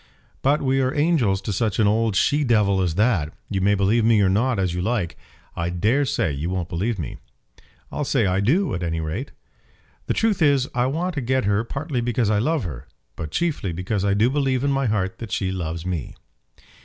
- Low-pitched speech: Yes, low, 105 Hz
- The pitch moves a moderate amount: No, wide, 6.0 semitones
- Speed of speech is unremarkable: No, fast, 215 wpm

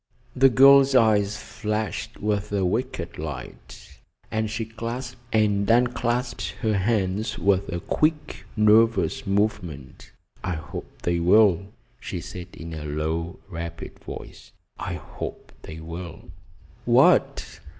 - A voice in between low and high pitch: No, low, 105 Hz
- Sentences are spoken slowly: Yes, slow, 120 wpm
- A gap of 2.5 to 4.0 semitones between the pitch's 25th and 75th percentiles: No, average, 5.1 semitones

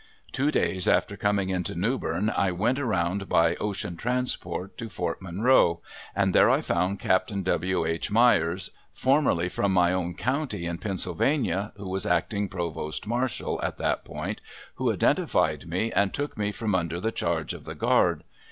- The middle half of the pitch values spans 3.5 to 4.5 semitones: Yes, average, 4.1 semitones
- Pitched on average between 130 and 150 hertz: No, very low, 95 Hz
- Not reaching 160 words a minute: No, average, 165 wpm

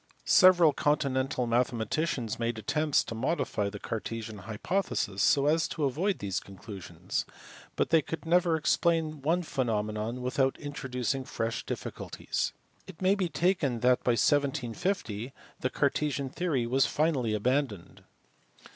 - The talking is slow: Yes, slow, 130 wpm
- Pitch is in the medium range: No, low, 130 Hz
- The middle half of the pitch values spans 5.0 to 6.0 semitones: Yes, wide, 5.6 semitones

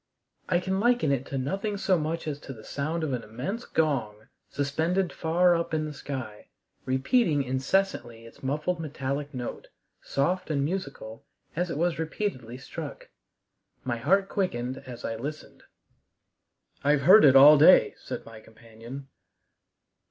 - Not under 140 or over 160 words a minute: Yes, average, 150 wpm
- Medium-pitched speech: Yes, medium, 145 Hz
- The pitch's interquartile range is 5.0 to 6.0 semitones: Yes, average, 5.3 semitones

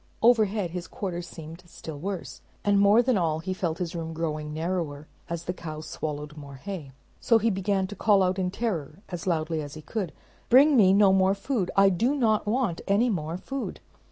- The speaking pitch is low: No, medium, 185 Hz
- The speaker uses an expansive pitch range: No, average, 4.2 semitones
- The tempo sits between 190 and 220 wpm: Yes, average, 200 wpm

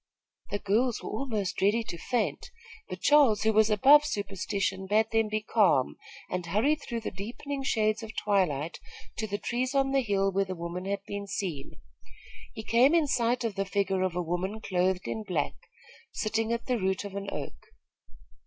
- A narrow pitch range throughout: No, average, 3.5 semitones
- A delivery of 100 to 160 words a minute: No, average, 185 wpm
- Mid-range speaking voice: No, high, 210 Hz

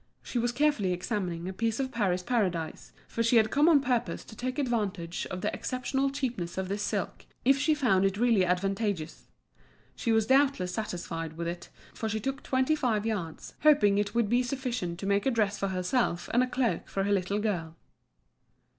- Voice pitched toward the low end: No, high, 215 Hz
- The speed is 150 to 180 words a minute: No, average, 195 wpm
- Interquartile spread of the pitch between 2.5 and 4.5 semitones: No, average, 5.3 semitones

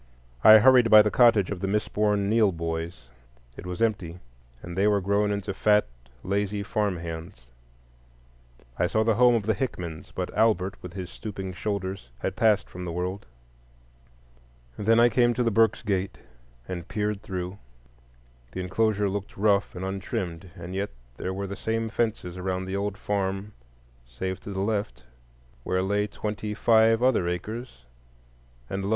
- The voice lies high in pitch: No, low, 100 Hz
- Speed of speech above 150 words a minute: Yes, average, 165 wpm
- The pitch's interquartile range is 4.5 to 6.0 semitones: No, average, 2.7 semitones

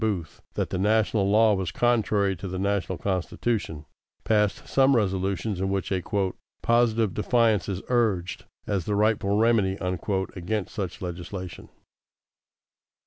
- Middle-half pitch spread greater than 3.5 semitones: No, average, 2.8 semitones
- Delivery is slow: Yes, slow, 130 wpm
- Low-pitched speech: Yes, low, 100 Hz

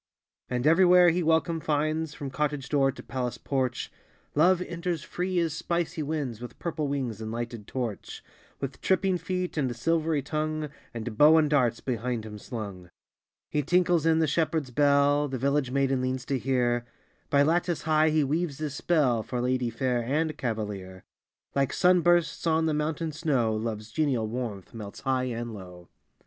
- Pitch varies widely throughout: No, average, 4.8 semitones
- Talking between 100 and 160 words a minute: No, average, 175 wpm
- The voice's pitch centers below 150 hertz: Yes, medium, 140 Hz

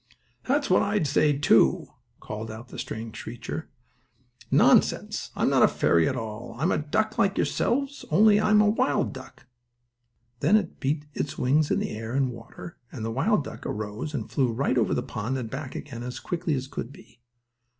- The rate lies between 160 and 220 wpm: Yes, average, 185 wpm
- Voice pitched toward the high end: No, low, 135 Hz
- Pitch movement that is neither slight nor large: No, wide, 6.6 semitones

